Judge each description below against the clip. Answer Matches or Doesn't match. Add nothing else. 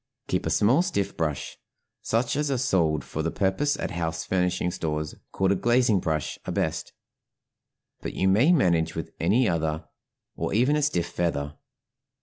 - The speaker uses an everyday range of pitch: Doesn't match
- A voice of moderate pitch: Doesn't match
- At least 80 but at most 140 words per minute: Doesn't match